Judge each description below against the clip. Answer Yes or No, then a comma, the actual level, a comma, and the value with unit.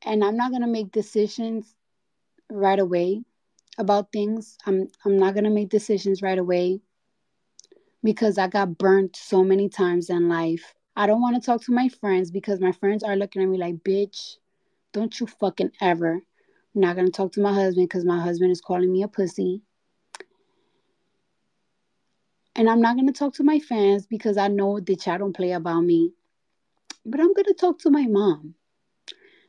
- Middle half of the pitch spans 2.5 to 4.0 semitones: Yes, average, 3.3 semitones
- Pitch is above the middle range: Yes, high, 200 Hz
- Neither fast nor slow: Yes, average, 185 wpm